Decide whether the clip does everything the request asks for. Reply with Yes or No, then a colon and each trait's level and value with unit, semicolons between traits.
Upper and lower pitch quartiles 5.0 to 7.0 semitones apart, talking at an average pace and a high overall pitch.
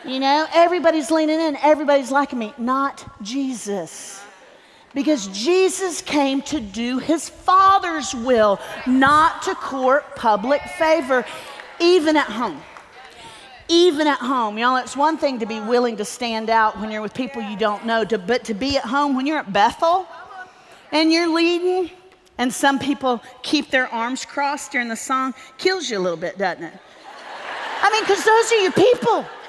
Yes: wide, 5.4 semitones; average, 170 wpm; very high, 275 Hz